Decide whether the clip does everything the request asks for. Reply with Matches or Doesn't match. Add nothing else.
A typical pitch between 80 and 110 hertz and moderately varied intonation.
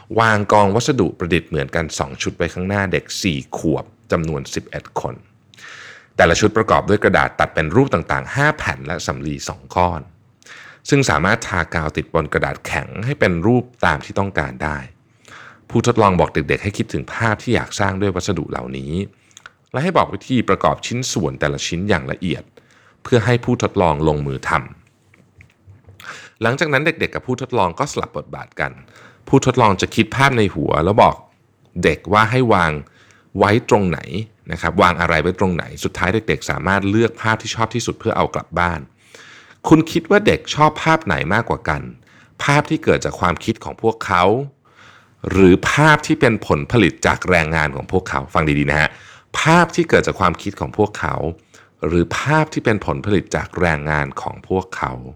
Doesn't match